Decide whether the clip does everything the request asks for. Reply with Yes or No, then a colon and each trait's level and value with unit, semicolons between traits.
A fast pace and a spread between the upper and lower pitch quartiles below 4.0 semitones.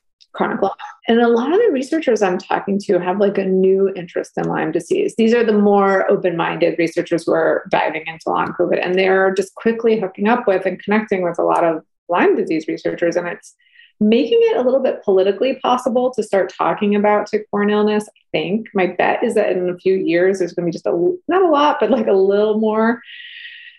No: fast, 215 wpm; average, 4.6 semitones